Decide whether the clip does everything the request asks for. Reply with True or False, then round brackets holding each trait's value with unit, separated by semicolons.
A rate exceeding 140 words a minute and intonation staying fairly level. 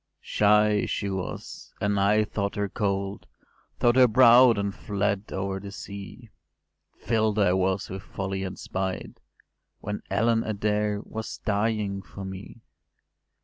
False (135 wpm; 1.7 semitones)